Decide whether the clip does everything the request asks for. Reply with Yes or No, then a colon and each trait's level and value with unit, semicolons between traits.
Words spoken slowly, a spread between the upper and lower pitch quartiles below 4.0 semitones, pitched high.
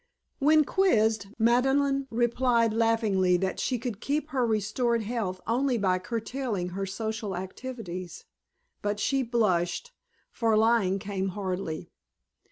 No: slow, 120 wpm; average, 4.3 semitones; high, 225 Hz